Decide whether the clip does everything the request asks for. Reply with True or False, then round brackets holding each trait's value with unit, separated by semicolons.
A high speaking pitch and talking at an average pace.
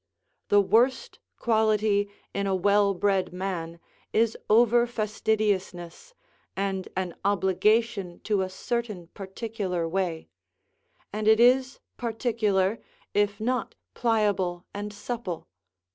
False (205 Hz; 105 wpm)